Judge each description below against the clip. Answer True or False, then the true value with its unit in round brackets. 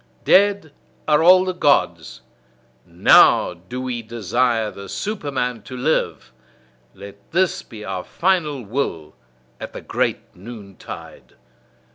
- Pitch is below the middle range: True (125 Hz)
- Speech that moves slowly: True (115 wpm)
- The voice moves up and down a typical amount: False (7.7 semitones)